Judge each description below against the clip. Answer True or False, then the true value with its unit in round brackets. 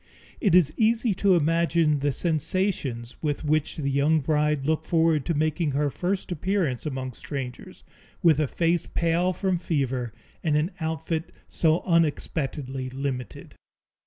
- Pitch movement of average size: True (3.3 semitones)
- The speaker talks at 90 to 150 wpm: True (140 wpm)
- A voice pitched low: False (155 Hz)